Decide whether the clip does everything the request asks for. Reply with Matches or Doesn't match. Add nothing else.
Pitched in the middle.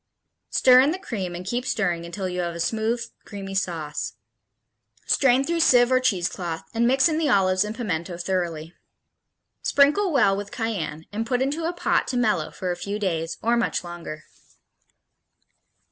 Doesn't match